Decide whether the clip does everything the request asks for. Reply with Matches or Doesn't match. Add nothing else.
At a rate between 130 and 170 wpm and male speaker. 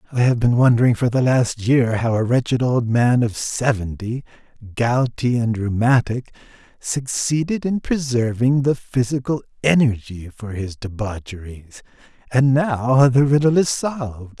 Matches